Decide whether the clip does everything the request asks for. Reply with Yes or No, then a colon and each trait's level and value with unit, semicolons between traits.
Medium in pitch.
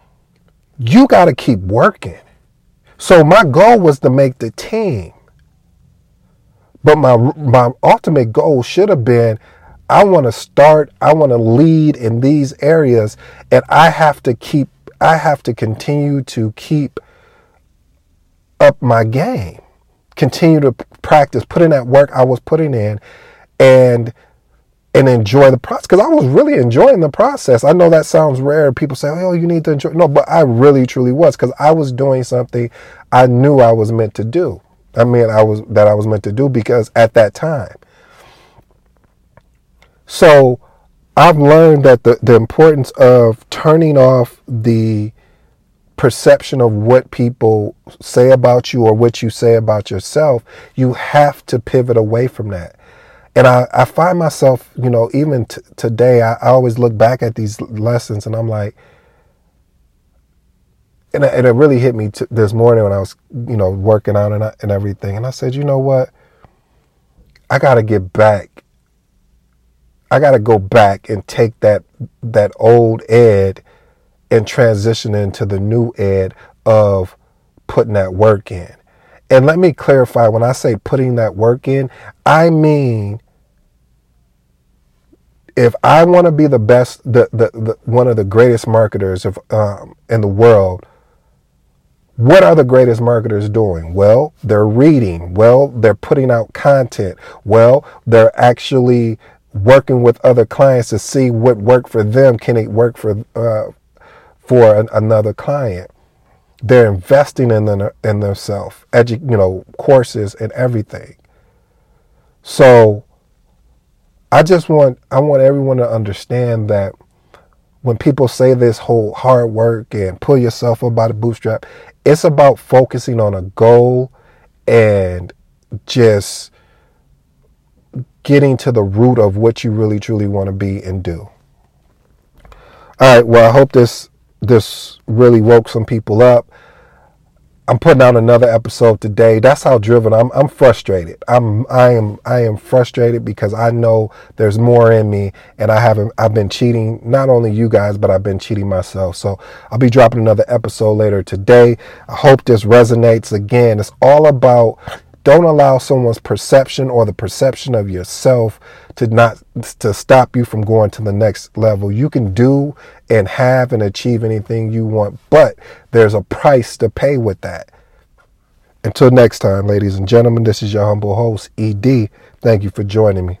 No: low, 115 Hz